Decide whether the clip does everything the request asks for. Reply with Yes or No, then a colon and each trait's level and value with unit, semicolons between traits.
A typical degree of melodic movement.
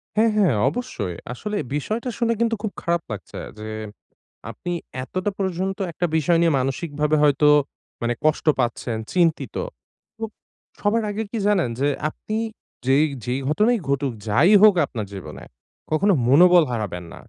No: wide, 7.5 semitones